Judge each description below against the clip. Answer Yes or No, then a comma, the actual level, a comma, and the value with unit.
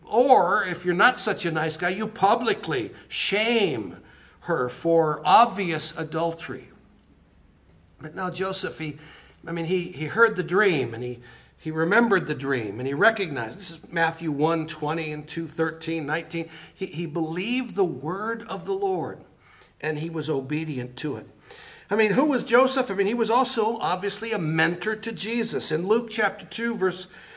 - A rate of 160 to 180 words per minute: Yes, average, 170 wpm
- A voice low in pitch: No, medium, 175 Hz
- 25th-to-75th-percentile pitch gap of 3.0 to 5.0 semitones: No, wide, 5.5 semitones